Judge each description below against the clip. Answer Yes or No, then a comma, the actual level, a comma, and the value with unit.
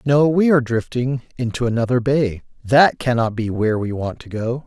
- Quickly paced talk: No, average, 195 wpm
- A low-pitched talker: Yes, low, 125 Hz